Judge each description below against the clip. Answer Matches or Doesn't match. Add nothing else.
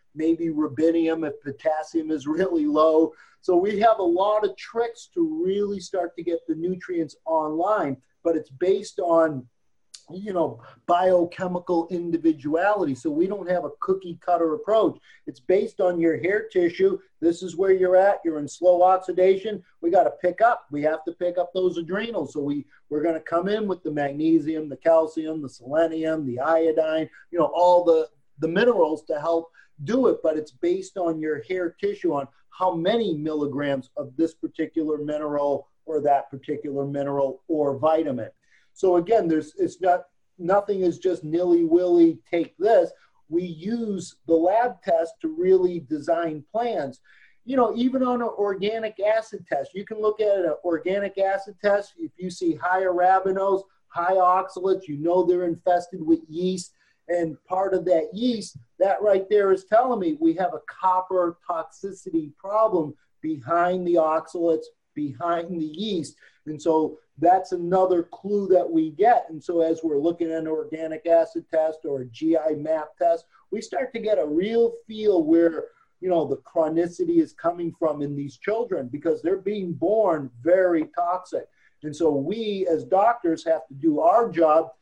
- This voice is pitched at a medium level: Matches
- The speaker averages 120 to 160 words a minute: Doesn't match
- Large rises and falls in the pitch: Doesn't match